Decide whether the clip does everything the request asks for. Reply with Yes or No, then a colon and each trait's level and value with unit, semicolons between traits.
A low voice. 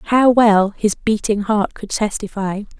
No: high, 210 Hz